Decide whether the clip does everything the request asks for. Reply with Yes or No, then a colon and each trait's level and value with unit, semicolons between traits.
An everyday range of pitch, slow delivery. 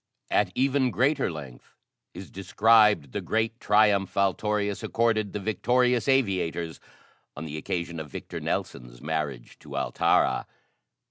No: wide, 5.8 semitones; slow, 125 wpm